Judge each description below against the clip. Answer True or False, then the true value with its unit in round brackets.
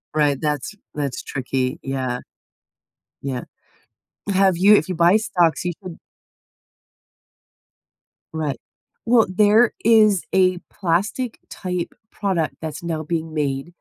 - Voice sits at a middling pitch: True (170 Hz)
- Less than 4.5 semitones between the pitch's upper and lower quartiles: False (4.8 semitones)